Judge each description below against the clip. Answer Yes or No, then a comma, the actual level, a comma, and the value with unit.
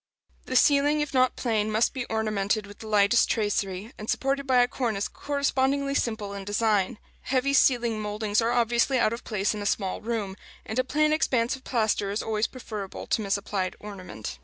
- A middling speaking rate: Yes, average, 185 wpm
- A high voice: Yes, high, 220 Hz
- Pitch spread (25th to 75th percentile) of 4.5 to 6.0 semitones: No, average, 3.8 semitones